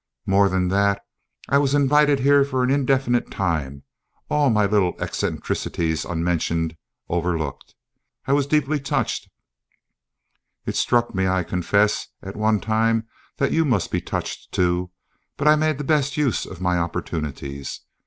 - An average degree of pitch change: No, wide, 7.8 semitones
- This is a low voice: Yes, low, 105 Hz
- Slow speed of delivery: No, average, 145 wpm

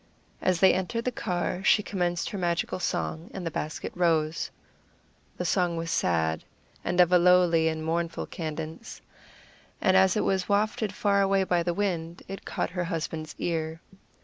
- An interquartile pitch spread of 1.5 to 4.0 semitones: Yes, narrow, 2.6 semitones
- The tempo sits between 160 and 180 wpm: Yes, average, 170 wpm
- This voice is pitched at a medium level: Yes, medium, 175 Hz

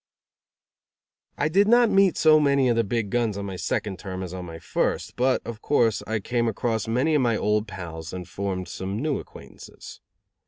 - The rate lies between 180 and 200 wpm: Yes, average, 195 wpm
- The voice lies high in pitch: No, low, 110 Hz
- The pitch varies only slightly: No, wide, 5.6 semitones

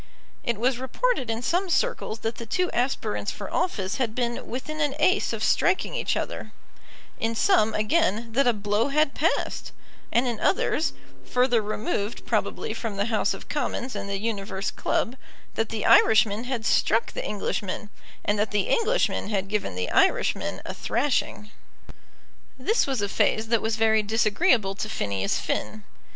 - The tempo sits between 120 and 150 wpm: No, average, 165 wpm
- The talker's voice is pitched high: Yes, high, 225 Hz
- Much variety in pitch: No, average, 3.9 semitones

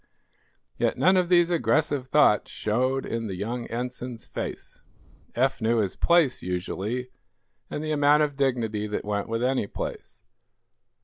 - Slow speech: No, average, 145 wpm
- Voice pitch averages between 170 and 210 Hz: No, low, 125 Hz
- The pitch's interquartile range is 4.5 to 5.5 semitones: Yes, average, 4.8 semitones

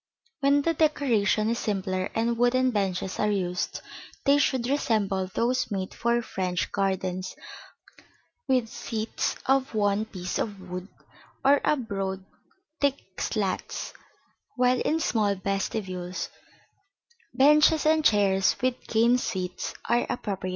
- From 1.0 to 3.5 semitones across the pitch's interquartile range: No, average, 5.0 semitones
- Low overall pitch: No, high, 215 Hz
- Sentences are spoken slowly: Yes, slow, 125 wpm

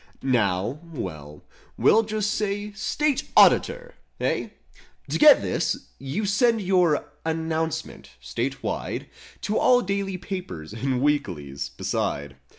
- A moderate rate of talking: No, slow, 115 wpm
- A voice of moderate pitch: Yes, medium, 165 Hz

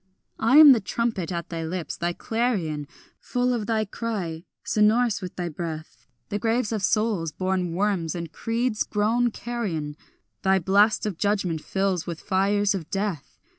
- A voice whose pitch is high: Yes, high, 200 Hz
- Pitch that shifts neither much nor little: Yes, average, 4.6 semitones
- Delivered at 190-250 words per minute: No, average, 160 wpm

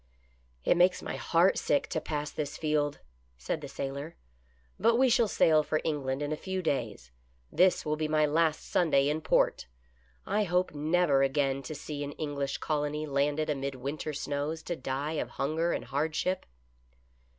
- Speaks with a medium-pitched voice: Yes, medium, 150 Hz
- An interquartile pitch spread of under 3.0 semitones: Yes, narrow, 2.4 semitones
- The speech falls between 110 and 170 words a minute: No, average, 180 wpm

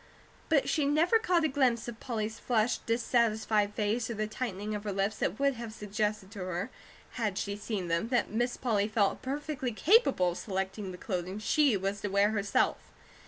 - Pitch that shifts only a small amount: No, average, 3.5 semitones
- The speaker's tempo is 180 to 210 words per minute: Yes, average, 190 wpm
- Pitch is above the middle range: Yes, high, 215 Hz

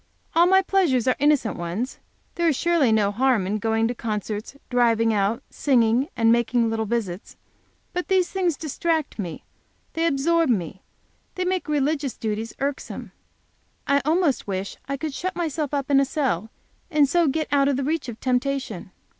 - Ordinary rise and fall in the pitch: No, wide, 5.7 semitones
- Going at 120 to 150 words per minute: No, average, 170 wpm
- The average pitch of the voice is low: No, very high, 270 Hz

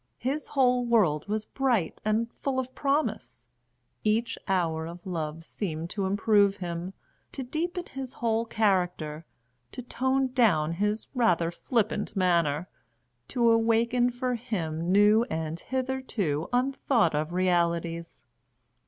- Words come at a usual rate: No, slow, 125 wpm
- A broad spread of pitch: Yes, wide, 6.5 semitones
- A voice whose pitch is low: No, high, 210 Hz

